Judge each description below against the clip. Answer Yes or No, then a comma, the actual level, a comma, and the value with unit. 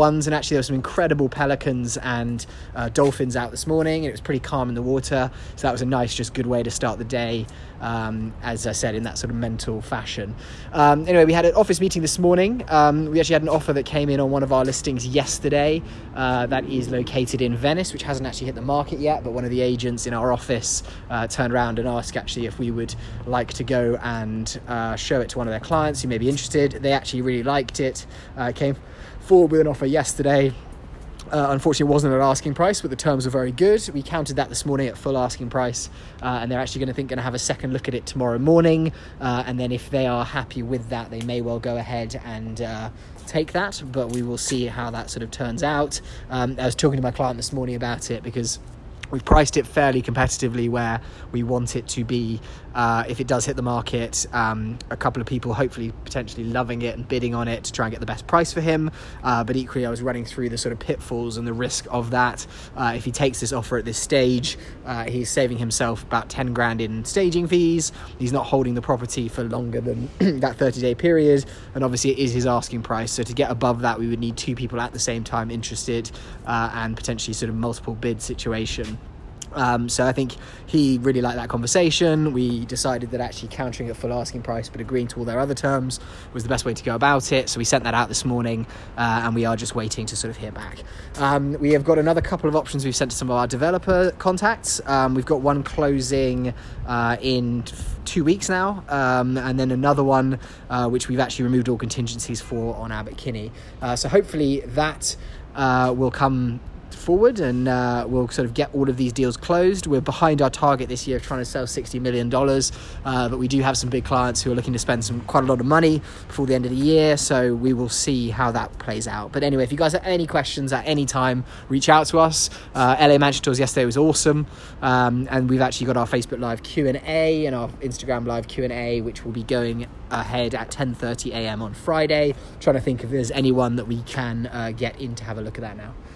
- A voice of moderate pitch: No, low, 125 Hz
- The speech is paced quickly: Yes, fast, 240 wpm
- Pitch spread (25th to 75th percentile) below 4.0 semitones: Yes, average, 2.8 semitones